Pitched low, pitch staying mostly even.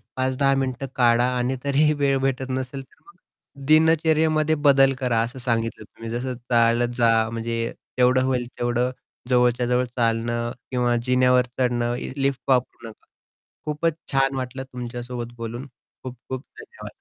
Yes: low, 125 Hz; narrow, 2.2 semitones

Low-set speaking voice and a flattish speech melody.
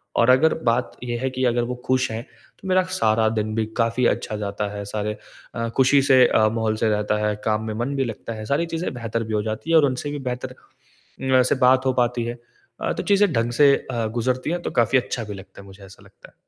No: low, 120 Hz; average, 3.1 semitones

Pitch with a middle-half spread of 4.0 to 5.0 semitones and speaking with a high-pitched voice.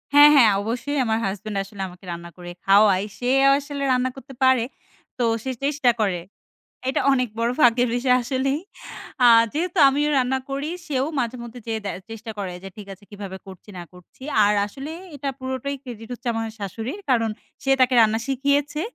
Yes: average, 4.5 semitones; high, 245 Hz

